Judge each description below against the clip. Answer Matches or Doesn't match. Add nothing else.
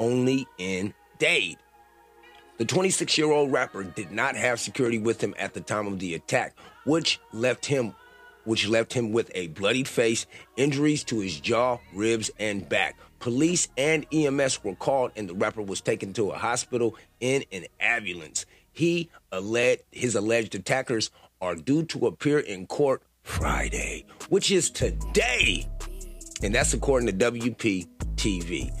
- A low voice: Matches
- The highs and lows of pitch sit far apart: Matches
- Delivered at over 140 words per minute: Matches